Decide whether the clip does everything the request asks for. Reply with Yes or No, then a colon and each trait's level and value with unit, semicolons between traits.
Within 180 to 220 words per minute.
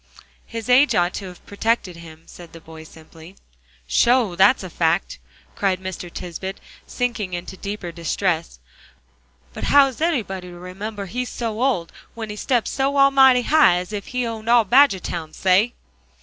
No: average, 165 wpm